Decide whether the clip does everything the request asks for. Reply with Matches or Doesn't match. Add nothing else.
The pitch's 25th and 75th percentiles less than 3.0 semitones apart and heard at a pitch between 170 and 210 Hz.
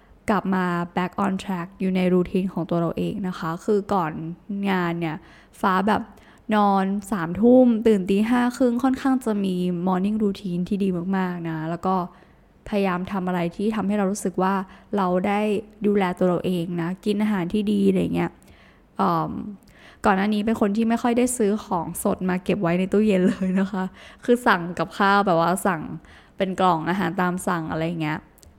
Matches